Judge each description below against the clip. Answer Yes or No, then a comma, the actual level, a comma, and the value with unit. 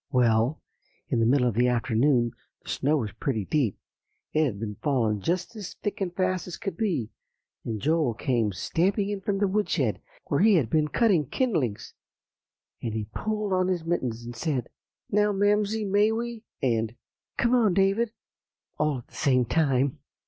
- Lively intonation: Yes, wide, 8.9 semitones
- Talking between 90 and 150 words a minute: No, average, 175 wpm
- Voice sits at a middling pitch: Yes, medium, 155 Hz